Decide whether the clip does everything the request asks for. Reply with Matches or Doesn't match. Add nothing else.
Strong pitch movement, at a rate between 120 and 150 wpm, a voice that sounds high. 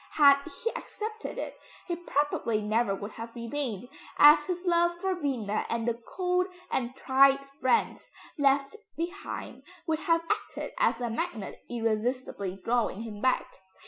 Matches